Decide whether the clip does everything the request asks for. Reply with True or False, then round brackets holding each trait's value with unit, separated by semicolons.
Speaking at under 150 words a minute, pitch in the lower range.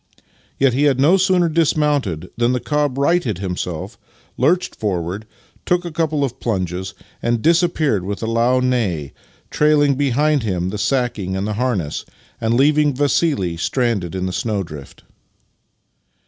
True (140 wpm; 125 Hz)